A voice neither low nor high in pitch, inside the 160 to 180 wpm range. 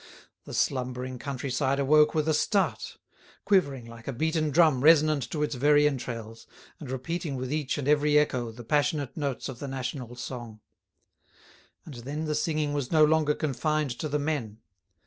Yes: medium, 145 Hz; average, 165 wpm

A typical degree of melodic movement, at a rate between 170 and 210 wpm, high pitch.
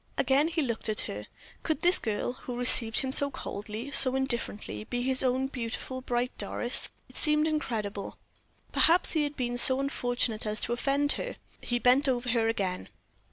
Yes: average, 3.2 semitones; average, 175 wpm; very high, 250 Hz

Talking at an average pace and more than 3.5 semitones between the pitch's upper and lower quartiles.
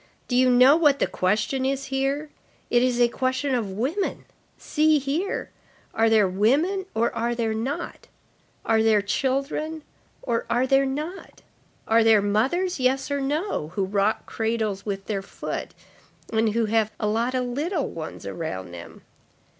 Yes: average, 160 wpm; average, 4.1 semitones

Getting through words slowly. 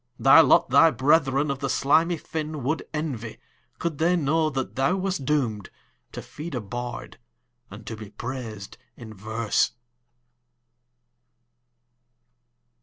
Yes: slow, 125 wpm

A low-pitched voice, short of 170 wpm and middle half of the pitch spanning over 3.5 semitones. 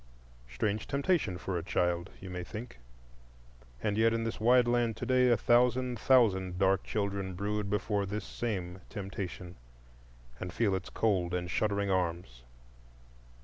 Yes: low, 100 Hz; average, 145 wpm; average, 4.0 semitones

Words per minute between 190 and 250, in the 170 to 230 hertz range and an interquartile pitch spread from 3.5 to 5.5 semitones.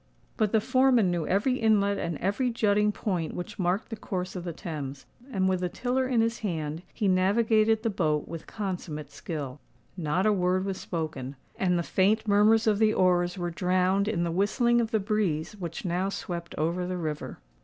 Yes: average, 195 wpm; medium, 185 Hz; average, 3.9 semitones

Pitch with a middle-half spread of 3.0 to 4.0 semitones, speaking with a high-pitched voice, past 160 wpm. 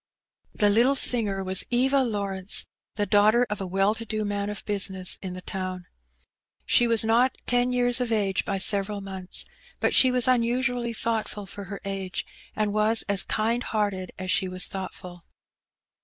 Yes: average, 3.3 semitones; high, 205 Hz; average, 170 wpm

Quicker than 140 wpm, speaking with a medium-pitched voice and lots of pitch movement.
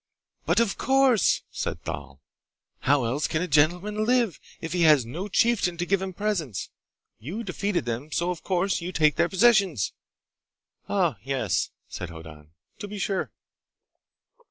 Yes: average, 155 wpm; medium, 175 Hz; wide, 6.3 semitones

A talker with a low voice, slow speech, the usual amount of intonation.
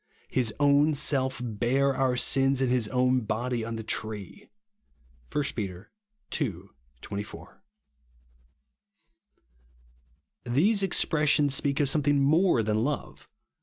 Yes: low, 130 Hz; slow, 110 wpm; average, 4.1 semitones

